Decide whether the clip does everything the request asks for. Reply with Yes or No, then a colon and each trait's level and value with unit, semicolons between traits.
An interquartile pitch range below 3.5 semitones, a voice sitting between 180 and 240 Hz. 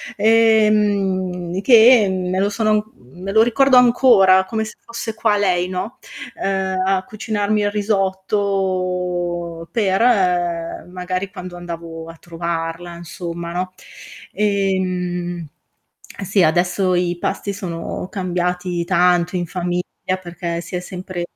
Yes: narrow, 2.6 semitones; medium, 185 Hz